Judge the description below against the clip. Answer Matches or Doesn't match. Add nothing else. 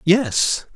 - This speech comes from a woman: Doesn't match